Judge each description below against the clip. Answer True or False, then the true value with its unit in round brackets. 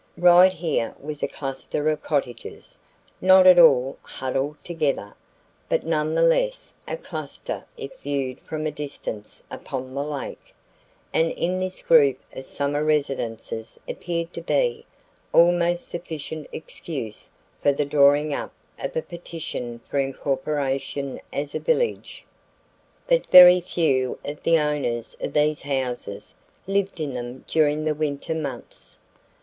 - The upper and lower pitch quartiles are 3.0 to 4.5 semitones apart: True (3.8 semitones)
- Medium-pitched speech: True (150 Hz)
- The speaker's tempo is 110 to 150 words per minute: True (135 wpm)